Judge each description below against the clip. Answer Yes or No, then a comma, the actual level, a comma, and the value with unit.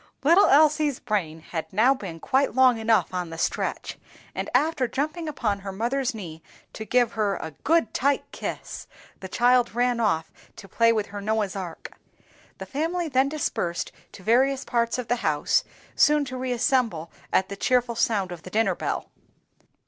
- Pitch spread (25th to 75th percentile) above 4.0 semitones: Yes, average, 5.3 semitones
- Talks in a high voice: Yes, high, 235 Hz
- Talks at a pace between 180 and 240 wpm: No, average, 170 wpm